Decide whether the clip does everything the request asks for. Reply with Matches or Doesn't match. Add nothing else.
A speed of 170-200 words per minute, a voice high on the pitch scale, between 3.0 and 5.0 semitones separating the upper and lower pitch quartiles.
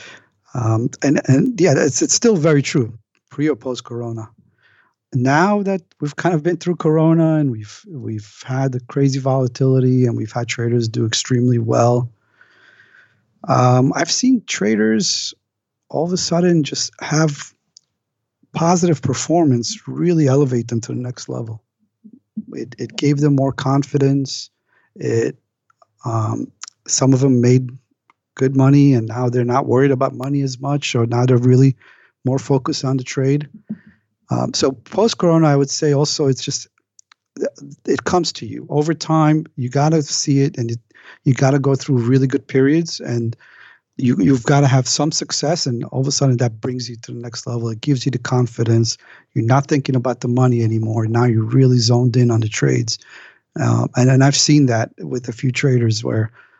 Doesn't match